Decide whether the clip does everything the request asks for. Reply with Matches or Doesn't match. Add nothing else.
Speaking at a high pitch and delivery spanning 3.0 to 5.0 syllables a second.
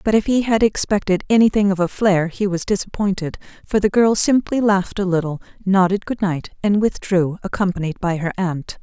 Doesn't match